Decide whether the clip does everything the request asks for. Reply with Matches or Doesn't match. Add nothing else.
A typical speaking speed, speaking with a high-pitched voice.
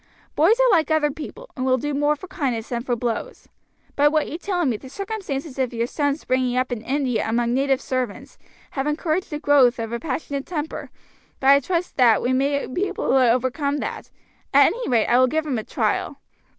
Doesn't match